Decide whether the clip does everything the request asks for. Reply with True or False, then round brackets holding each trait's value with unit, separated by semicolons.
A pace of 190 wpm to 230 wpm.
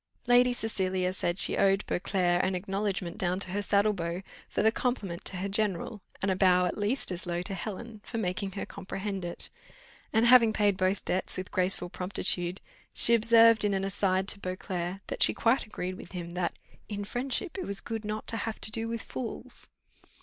True (200 wpm)